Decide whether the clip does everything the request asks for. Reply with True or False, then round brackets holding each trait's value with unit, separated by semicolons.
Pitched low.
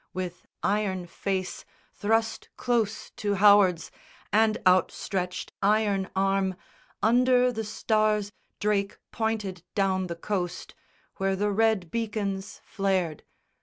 False (200 Hz)